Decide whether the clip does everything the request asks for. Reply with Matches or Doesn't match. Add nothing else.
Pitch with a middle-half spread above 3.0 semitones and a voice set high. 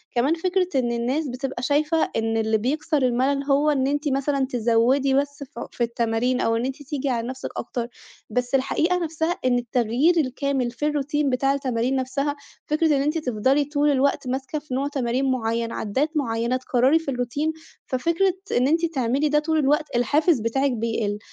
Matches